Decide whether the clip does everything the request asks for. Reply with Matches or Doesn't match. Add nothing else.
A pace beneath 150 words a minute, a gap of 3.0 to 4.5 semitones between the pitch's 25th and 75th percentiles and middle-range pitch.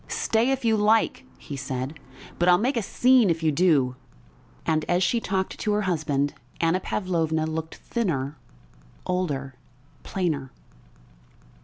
Doesn't match